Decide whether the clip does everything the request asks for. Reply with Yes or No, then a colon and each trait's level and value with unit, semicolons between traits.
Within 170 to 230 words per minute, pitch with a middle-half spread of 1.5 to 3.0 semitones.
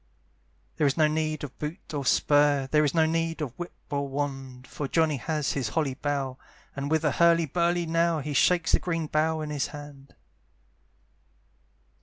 Yes: average, 180 wpm; narrow, 2.5 semitones